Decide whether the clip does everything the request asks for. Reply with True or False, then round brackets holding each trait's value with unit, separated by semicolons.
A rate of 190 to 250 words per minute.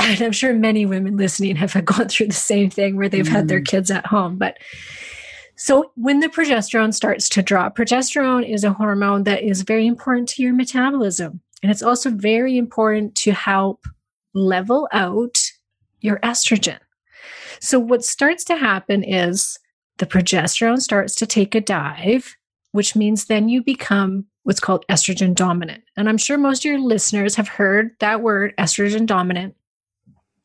False (165 wpm)